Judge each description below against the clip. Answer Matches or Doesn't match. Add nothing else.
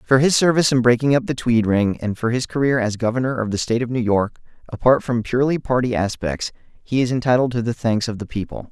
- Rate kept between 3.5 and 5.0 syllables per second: Doesn't match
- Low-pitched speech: Matches